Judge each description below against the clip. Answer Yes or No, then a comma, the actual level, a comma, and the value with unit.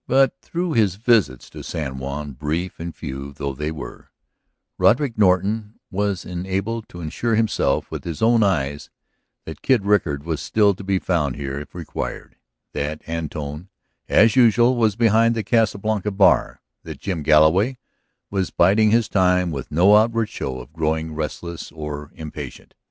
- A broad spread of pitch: Yes, wide, 6.2 semitones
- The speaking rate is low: No, average, 160 wpm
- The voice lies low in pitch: Yes, very low, 90 Hz